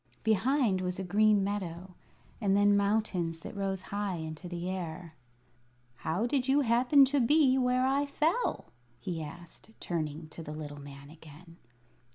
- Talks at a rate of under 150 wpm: No, average, 155 wpm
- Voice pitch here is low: No, high, 190 Hz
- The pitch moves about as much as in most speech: No, wide, 6.2 semitones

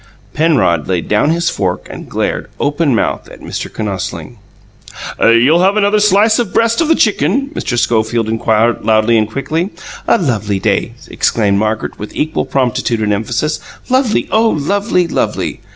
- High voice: No, low, 135 Hz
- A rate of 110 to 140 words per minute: No, average, 155 wpm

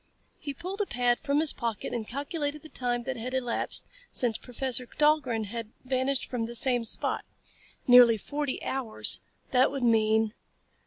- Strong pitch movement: No, average, 3.1 semitones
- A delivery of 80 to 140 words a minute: No, average, 160 wpm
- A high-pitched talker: Yes, very high, 250 Hz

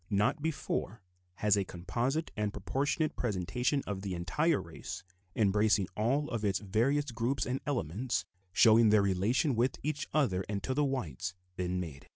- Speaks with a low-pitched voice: Yes, low, 110 Hz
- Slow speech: No, average, 160 wpm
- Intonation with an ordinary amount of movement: No, wide, 5.9 semitones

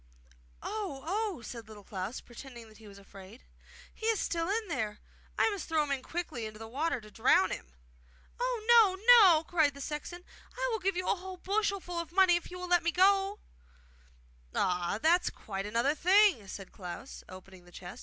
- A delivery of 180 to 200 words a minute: Yes, average, 195 wpm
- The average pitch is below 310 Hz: No, very high, 320 Hz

